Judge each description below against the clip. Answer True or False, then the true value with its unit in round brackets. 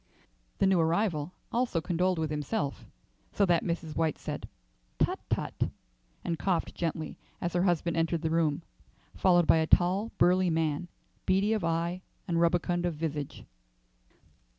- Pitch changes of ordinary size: False (2.1 semitones)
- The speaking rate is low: False (150 wpm)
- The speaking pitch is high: False (170 Hz)